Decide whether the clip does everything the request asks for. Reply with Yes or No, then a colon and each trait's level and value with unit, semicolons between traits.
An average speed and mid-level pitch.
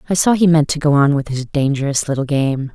No: fast, 265 wpm; medium, 145 Hz